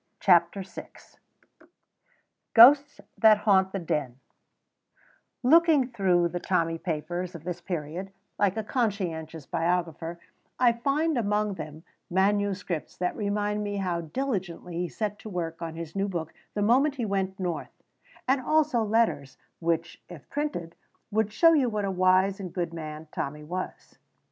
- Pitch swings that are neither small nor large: Yes, average, 4.2 semitones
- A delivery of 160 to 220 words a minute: No, average, 145 wpm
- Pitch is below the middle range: No, high, 190 Hz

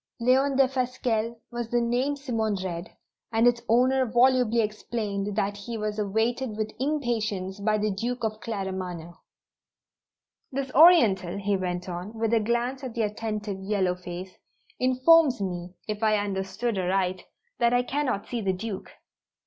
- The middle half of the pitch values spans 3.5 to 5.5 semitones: Yes, average, 3.8 semitones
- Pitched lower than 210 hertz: No, high, 220 Hz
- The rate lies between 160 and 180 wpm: No, average, 150 wpm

